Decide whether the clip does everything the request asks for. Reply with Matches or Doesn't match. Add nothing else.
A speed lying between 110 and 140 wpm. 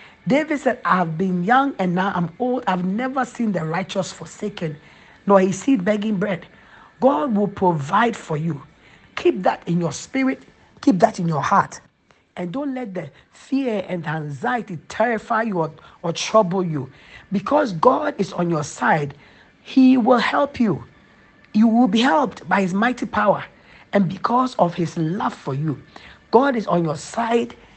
Doesn't match